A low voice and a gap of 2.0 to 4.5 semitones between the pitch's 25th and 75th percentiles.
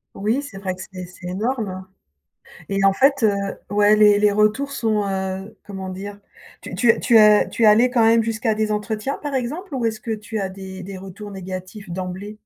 No: high, 210 Hz; average, 2.8 semitones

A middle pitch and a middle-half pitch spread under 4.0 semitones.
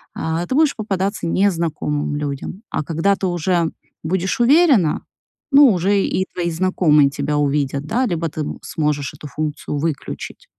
No: medium, 170 Hz; average, 4.7 semitones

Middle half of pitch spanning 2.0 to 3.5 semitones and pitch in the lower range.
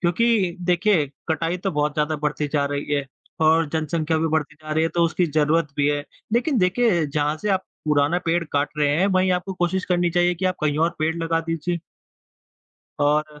No: average, 2.9 semitones; medium, 165 Hz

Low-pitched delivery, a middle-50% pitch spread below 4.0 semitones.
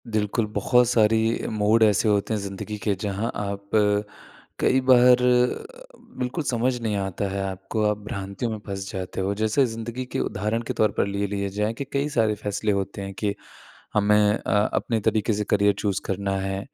Yes: low, 105 Hz; narrow, 2.4 semitones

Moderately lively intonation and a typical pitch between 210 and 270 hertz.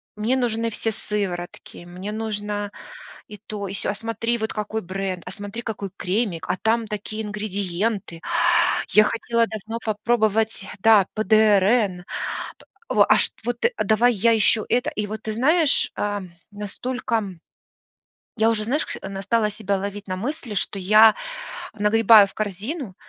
No: narrow, 2.1 semitones; high, 215 Hz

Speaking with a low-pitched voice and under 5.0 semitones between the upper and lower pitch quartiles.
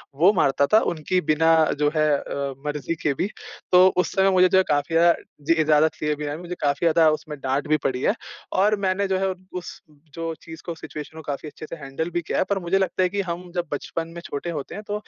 No: medium, 165 Hz; average, 3.5 semitones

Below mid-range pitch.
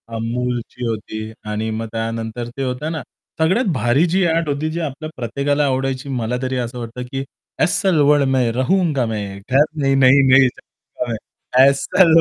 Yes: low, 130 Hz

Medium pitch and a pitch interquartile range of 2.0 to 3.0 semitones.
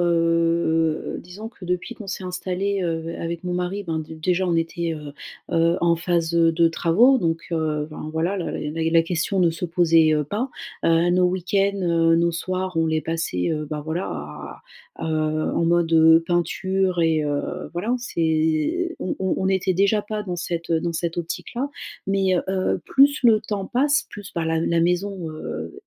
Yes: medium, 170 Hz; narrow, 2.5 semitones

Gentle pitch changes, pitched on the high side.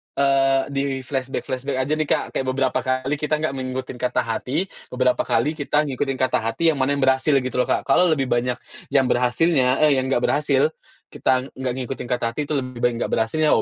No: narrow, 1.9 semitones; low, 130 Hz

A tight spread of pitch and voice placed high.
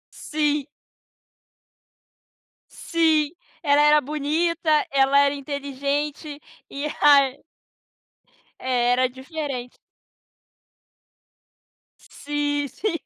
Yes: narrow, 1.5 semitones; very high, 290 Hz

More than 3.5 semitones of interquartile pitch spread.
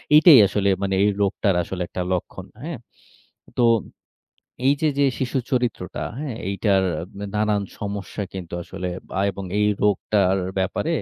Yes: average, 4.3 semitones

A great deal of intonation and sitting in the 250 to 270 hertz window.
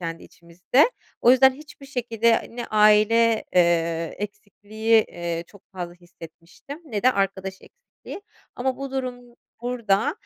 No: wide, 5.8 semitones; high, 215 Hz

